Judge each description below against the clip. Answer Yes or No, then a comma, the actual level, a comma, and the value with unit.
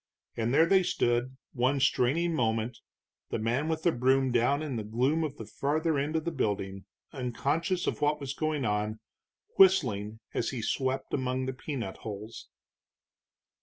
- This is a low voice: Yes, low, 130 Hz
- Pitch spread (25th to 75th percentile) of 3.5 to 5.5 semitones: Yes, average, 4.8 semitones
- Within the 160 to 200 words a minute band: Yes, average, 165 wpm